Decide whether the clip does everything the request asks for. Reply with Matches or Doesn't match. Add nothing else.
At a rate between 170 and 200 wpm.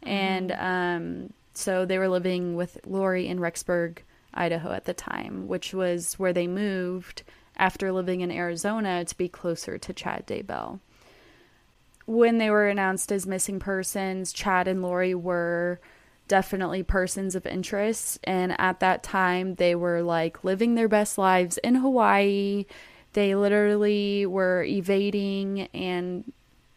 Doesn't match